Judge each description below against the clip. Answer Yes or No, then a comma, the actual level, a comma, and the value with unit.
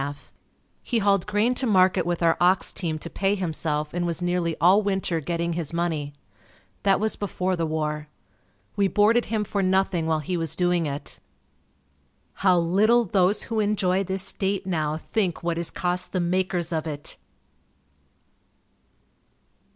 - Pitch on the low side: No, medium, 180 Hz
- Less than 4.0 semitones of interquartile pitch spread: Yes, average, 3.0 semitones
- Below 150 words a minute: No, average, 155 wpm